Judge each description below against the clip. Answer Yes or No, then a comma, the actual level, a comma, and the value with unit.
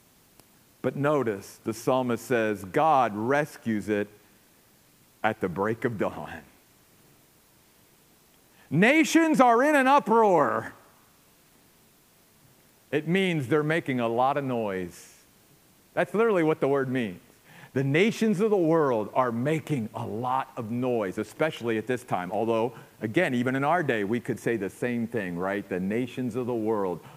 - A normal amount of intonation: No, wide, 5.7 semitones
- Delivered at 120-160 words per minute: Yes, average, 145 wpm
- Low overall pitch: Yes, low, 130 Hz